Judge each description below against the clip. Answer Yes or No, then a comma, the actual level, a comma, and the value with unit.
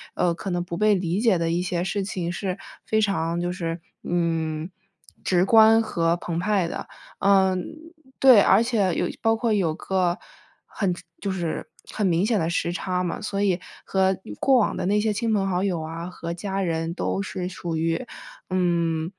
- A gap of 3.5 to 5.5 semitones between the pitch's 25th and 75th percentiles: No, average, 2.9 semitones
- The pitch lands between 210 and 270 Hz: No, medium, 185 Hz